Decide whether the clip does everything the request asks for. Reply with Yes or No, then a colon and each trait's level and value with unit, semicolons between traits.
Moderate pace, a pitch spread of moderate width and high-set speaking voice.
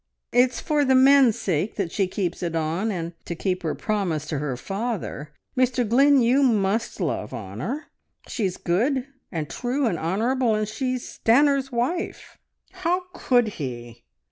No: average, 155 wpm; wide, 7.1 semitones; high, 220 Hz